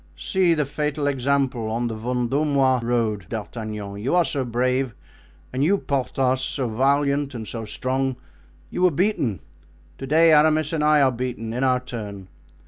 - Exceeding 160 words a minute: No, average, 150 wpm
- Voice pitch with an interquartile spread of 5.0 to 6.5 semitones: No, average, 3.7 semitones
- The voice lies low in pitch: Yes, low, 130 Hz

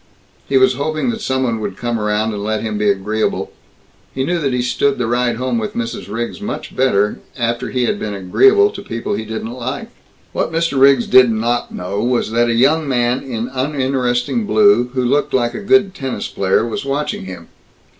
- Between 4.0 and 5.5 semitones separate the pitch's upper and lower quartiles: No, average, 3.6 semitones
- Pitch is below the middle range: Yes, low, 125 Hz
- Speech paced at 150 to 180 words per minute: No, fast, 205 wpm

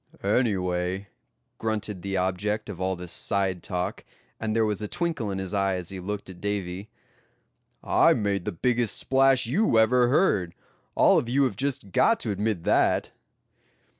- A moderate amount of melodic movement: Yes, average, 3.5 semitones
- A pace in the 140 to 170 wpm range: Yes, average, 165 wpm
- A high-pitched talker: No, low, 105 Hz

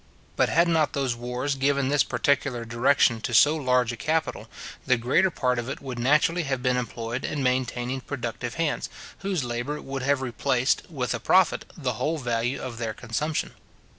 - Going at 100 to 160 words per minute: No, average, 180 wpm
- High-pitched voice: No, low, 130 Hz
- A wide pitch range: No, average, 3.0 semitones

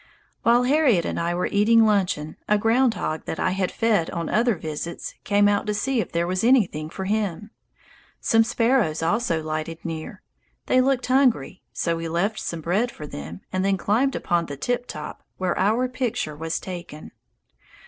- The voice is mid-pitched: No, high, 195 Hz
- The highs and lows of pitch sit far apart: Yes, wide, 5.7 semitones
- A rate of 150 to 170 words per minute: No, average, 180 wpm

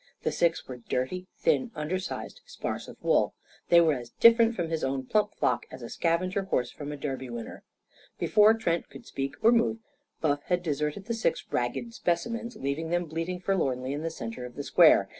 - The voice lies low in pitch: No, medium, 165 Hz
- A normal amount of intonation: No, wide, 6.0 semitones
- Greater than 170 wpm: Yes, average, 195 wpm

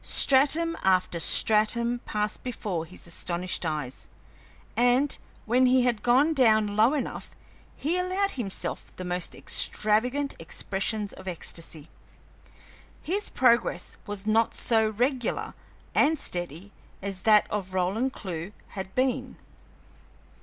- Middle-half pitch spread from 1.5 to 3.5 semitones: No, wide, 5.4 semitones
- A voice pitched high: Yes, high, 215 Hz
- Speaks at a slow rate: Yes, slow, 120 wpm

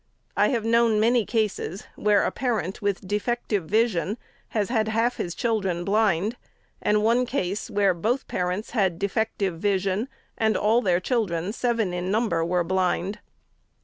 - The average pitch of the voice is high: Yes, high, 210 Hz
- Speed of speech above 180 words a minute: No, average, 150 wpm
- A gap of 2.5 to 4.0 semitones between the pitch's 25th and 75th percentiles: Yes, average, 3.5 semitones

